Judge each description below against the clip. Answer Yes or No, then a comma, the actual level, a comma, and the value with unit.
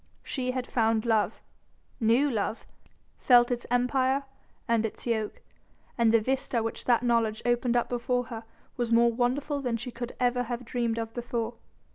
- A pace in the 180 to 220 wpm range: No, average, 165 wpm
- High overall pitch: Yes, high, 240 Hz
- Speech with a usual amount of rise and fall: No, narrow, 1.4 semitones